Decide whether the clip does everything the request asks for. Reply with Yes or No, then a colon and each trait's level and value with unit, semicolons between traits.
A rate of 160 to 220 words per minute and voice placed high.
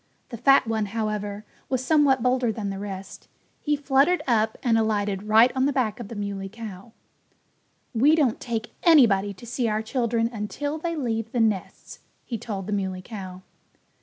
Yes: average, 175 wpm; high, 225 Hz